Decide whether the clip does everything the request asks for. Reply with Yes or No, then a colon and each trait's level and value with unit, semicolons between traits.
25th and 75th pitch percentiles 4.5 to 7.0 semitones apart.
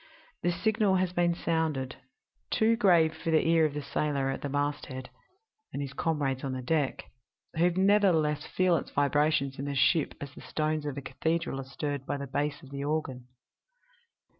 No: average, 3.3 semitones